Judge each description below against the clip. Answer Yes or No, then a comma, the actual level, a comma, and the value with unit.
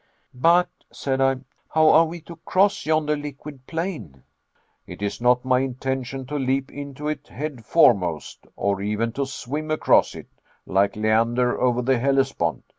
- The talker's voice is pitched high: No, low, 135 Hz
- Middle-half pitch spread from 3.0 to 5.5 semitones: Yes, average, 4.1 semitones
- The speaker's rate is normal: Yes, average, 155 wpm